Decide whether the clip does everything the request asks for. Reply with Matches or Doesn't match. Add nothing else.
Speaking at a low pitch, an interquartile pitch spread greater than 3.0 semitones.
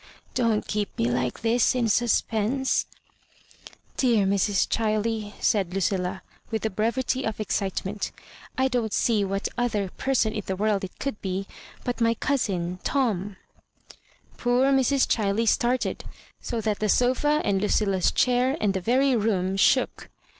Doesn't match